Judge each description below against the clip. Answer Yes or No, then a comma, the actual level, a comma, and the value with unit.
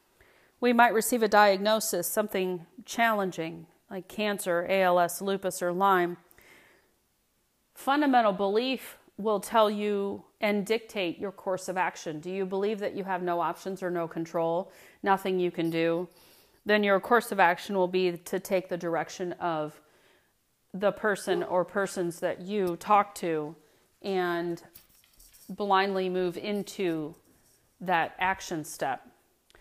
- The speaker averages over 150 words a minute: No, slow, 135 wpm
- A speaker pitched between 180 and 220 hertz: Yes, high, 190 Hz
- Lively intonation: No, average, 2.9 semitones